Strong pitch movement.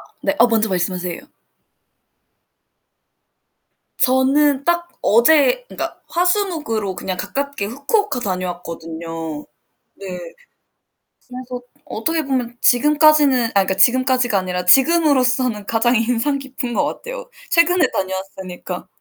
Yes: wide, 7.3 semitones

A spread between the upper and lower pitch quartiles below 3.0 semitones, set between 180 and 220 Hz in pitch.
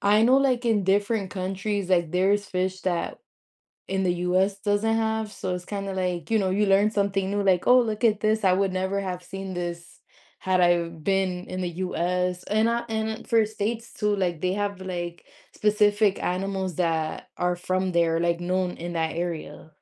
Yes: narrow, 2.5 semitones; high, 190 Hz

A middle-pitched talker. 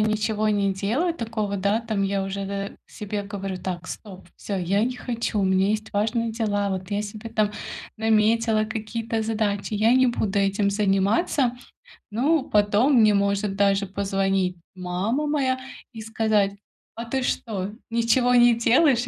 No: high, 210 Hz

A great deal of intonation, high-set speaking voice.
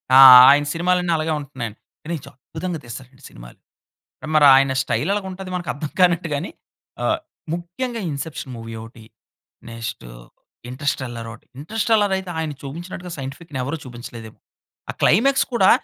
No: wide, 5.9 semitones; medium, 150 Hz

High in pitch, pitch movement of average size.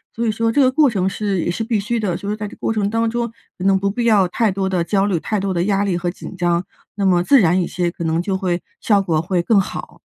Yes: high, 195 Hz; average, 3.4 semitones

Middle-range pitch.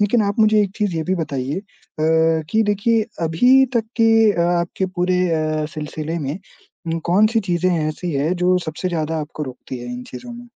Yes: medium, 175 Hz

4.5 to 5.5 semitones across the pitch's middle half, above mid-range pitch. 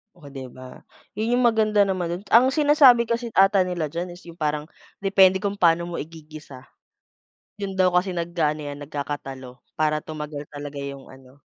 No: average, 5.1 semitones; medium, 170 Hz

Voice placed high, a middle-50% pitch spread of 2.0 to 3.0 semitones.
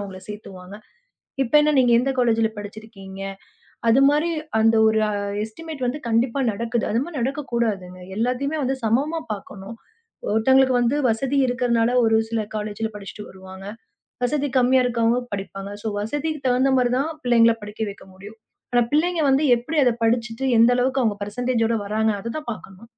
No: high, 230 Hz; average, 3.5 semitones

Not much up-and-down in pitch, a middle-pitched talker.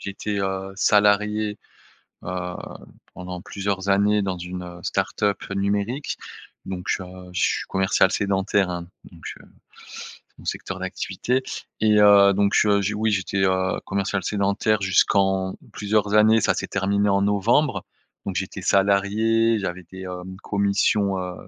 No: narrow, 1.5 semitones; low, 100 Hz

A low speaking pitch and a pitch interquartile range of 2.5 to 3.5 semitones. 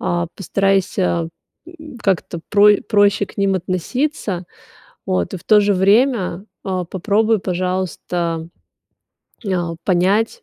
No: high, 190 Hz; average, 2.8 semitones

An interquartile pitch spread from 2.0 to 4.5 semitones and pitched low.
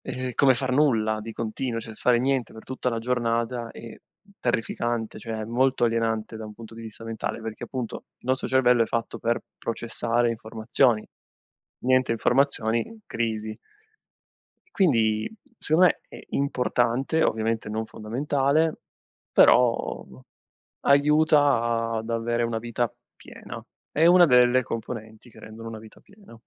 Yes: narrow, 2.5 semitones; low, 115 Hz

